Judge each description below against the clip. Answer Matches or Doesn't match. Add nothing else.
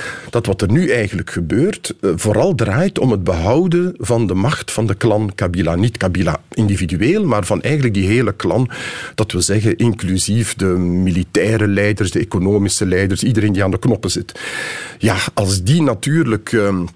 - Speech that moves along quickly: Doesn't match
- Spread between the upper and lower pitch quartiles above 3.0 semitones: Matches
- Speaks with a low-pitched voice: Matches